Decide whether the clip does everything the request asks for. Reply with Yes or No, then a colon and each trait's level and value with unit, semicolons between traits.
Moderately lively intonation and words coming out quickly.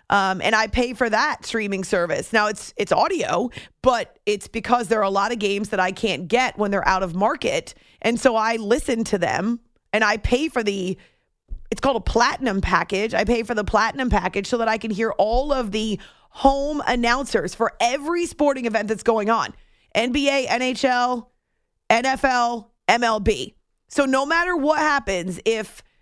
No: average, 3.4 semitones; average, 180 wpm